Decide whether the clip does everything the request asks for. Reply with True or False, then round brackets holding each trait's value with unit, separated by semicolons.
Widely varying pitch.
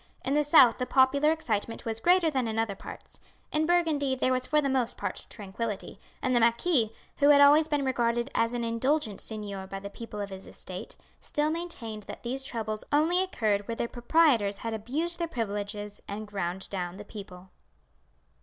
True (5.7 semitones)